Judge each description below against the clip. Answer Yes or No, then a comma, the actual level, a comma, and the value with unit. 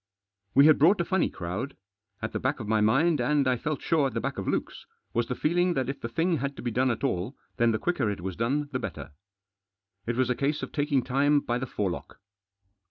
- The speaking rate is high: Yes, fast, 240 wpm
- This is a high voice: No, low, 130 Hz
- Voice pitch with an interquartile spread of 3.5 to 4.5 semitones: Yes, average, 4.1 semitones